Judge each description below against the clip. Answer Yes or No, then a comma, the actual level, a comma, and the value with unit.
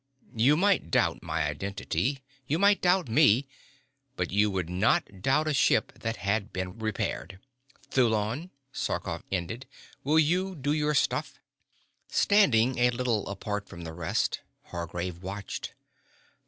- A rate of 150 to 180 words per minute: No, slow, 135 wpm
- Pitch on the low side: Yes, low, 110 Hz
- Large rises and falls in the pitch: Yes, wide, 7.3 semitones